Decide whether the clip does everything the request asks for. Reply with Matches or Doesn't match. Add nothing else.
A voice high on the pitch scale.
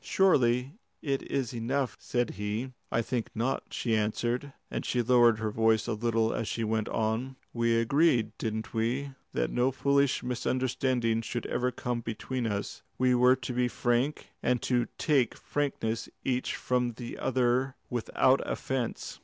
Doesn't match